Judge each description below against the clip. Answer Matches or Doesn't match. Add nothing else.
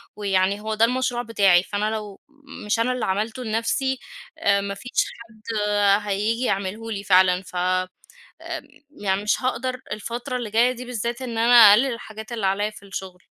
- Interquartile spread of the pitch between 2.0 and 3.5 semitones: Matches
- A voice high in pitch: Matches